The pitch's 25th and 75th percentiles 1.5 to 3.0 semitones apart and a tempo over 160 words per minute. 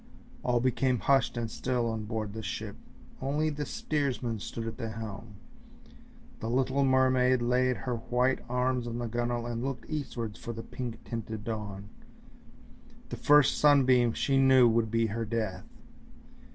No: narrow, 2.5 semitones; average, 155 wpm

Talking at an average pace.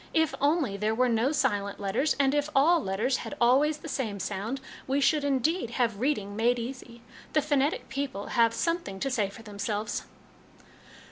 Yes: average, 180 wpm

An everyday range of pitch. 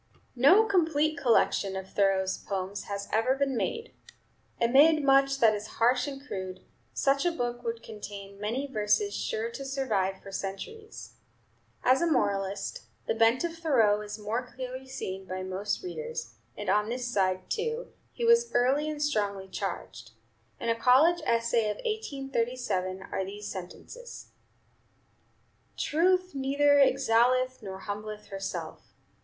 No: wide, 6.1 semitones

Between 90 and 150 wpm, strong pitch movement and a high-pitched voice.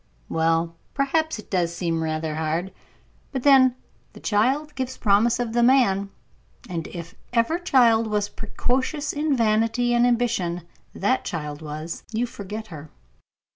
Yes: average, 140 wpm; wide, 6.6 semitones; high, 220 Hz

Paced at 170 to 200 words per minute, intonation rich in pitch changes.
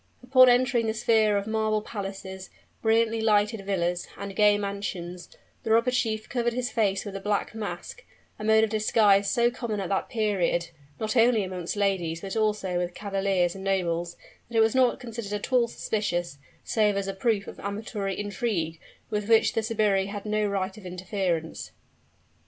No: average, 175 wpm; narrow, 2.5 semitones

